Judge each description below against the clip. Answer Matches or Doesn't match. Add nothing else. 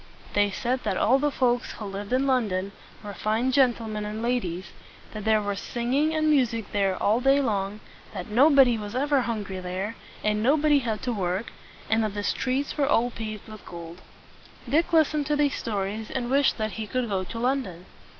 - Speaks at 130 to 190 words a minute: Doesn't match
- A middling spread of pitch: Matches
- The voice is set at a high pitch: Matches